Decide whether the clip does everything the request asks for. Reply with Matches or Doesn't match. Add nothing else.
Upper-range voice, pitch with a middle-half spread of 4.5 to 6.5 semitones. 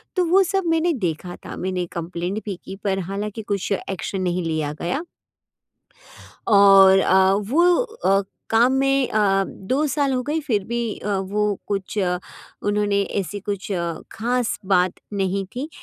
Matches